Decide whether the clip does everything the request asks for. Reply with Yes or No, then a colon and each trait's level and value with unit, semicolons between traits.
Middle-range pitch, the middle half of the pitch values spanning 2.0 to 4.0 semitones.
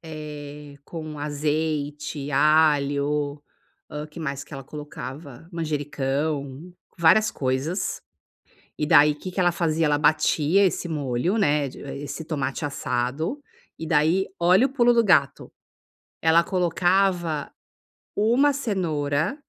Yes: medium, 150 Hz; average, 3.1 semitones